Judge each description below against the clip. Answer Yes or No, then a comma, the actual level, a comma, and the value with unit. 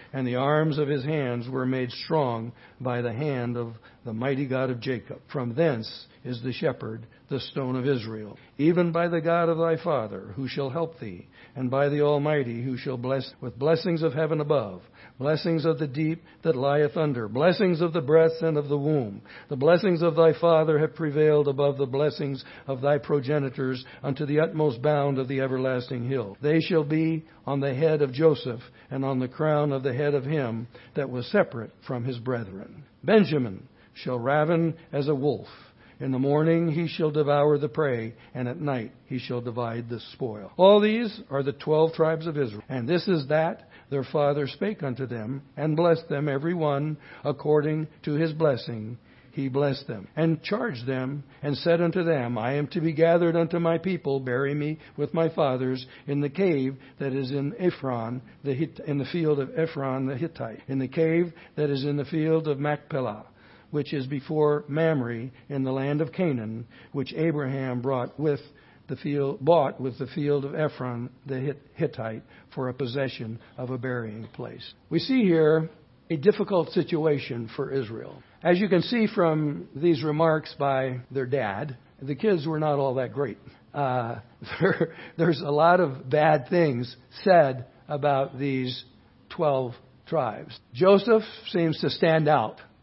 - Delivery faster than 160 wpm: Yes, average, 180 wpm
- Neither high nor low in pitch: Yes, medium, 145 Hz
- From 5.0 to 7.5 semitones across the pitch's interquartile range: No, average, 3.6 semitones